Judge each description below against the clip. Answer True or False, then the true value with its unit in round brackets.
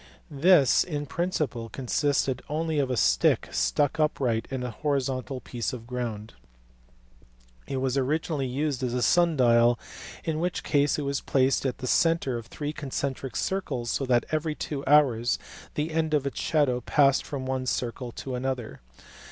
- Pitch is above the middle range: False (135 Hz)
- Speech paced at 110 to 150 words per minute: False (165 wpm)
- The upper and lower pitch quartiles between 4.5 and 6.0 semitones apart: False (3.2 semitones)